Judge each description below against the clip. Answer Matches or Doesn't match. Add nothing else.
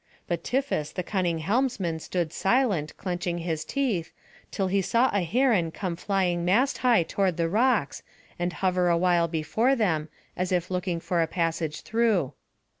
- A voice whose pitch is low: Doesn't match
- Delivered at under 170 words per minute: Matches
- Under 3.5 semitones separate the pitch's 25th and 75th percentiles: Doesn't match